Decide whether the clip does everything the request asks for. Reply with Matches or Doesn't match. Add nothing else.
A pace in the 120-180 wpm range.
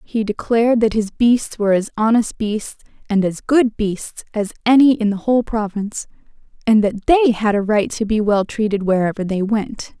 Doesn't match